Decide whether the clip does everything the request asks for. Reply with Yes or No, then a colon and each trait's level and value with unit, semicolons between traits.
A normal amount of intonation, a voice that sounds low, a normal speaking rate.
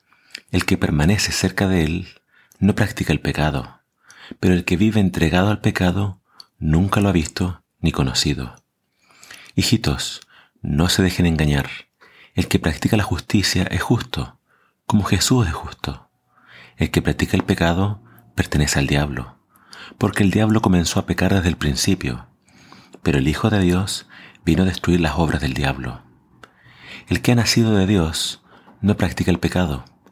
Yes: average, 3.9 semitones; very low, 90 Hz; average, 155 wpm